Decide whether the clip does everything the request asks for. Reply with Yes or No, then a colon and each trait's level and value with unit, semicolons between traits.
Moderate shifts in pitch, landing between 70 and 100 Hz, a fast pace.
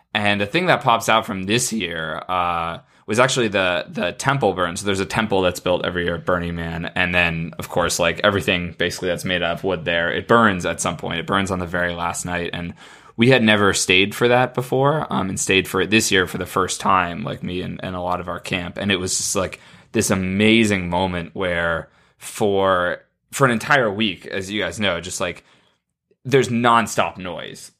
Yes: average, 3.6 semitones; very low, 95 Hz; fast, 220 wpm